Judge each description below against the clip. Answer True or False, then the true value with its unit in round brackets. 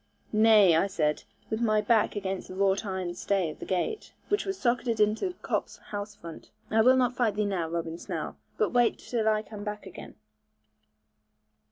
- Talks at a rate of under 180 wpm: False (185 wpm)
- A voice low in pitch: False (210 Hz)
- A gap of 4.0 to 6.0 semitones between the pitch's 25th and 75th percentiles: False (3.4 semitones)